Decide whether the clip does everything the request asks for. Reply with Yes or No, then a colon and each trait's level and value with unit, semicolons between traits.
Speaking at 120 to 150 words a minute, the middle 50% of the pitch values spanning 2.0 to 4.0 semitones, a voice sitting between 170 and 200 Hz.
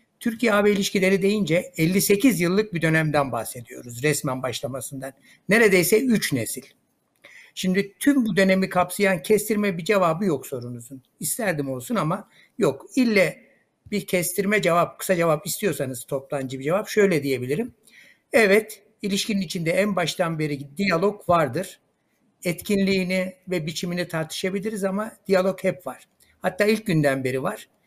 No: average, 130 wpm; average, 5.1 semitones; medium, 185 Hz